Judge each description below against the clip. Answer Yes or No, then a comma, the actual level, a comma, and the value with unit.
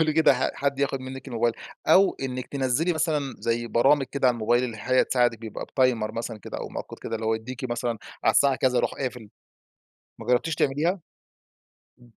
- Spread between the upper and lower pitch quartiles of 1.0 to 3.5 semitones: Yes, average, 2.9 semitones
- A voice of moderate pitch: No, low, 130 Hz